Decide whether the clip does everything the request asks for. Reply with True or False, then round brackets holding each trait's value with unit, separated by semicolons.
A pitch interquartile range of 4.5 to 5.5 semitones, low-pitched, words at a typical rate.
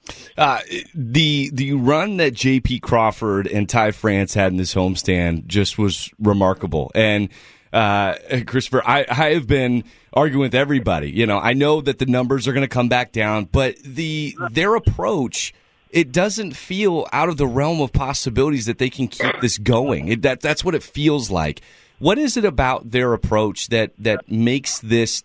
True (4.8 semitones; 125 Hz; 180 wpm)